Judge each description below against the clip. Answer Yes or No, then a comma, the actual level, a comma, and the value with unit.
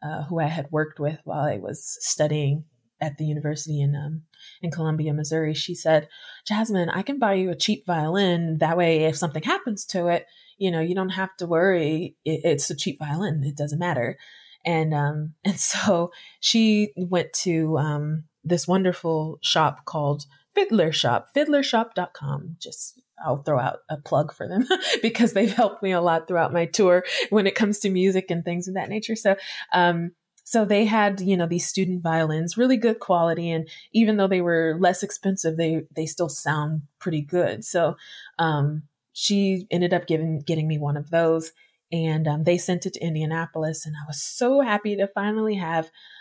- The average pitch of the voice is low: No, medium, 170 Hz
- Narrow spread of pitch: No, average, 3.7 semitones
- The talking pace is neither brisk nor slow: Yes, average, 190 wpm